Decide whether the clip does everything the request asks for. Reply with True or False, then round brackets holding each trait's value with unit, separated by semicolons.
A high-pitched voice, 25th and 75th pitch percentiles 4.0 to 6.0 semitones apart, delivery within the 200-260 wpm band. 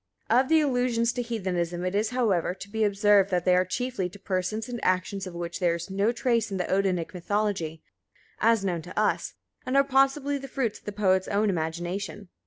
True (200 Hz; 4.3 semitones; 205 wpm)